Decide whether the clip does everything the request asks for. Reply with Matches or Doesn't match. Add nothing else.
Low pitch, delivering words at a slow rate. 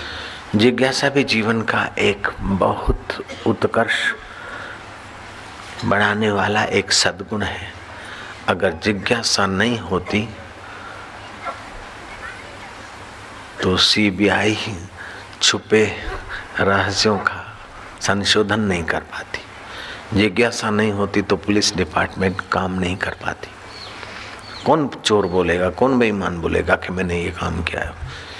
Matches